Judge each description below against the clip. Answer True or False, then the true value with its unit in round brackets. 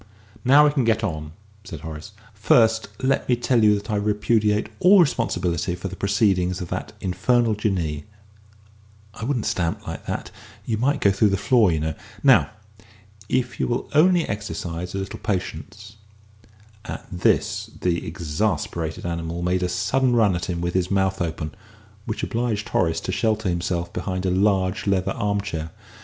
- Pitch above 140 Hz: False (100 Hz)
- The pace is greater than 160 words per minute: True (170 wpm)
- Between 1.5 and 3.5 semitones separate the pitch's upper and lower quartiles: False (4.1 semitones)